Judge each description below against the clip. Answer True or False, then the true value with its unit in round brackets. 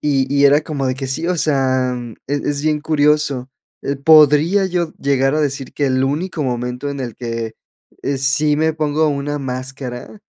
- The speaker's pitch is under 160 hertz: True (140 Hz)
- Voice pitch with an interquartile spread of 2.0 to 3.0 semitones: True (2.5 semitones)